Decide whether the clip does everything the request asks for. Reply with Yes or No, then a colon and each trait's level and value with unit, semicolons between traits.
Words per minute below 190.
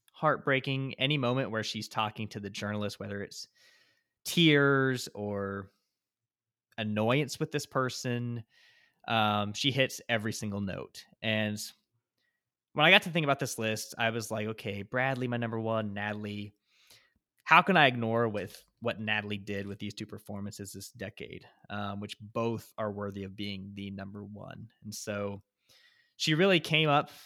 Yes: average, 155 wpm